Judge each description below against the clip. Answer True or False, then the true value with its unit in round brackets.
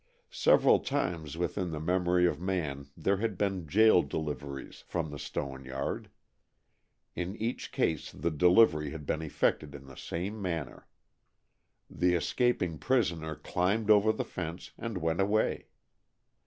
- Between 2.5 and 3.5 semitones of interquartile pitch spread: False (4.2 semitones)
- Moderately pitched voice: False (85 Hz)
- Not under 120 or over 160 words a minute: True (140 wpm)